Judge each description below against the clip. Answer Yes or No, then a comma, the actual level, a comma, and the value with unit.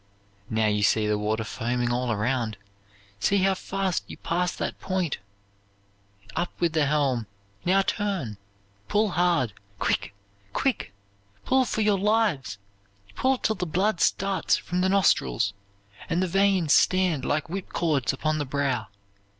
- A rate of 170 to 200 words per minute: No, average, 145 wpm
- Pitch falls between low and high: Yes, medium, 165 Hz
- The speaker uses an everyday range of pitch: No, wide, 7.8 semitones